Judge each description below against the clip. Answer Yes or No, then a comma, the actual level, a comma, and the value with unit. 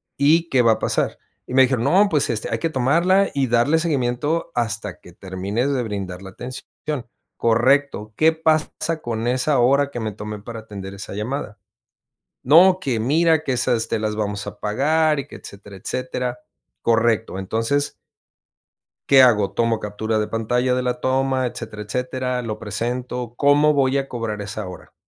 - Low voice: Yes, low, 125 Hz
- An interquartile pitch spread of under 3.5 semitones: No, average, 4.5 semitones